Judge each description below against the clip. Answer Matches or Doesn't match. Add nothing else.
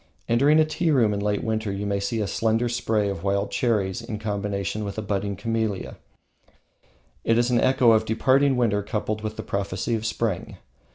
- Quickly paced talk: Doesn't match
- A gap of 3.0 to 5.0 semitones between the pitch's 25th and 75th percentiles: Doesn't match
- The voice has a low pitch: Matches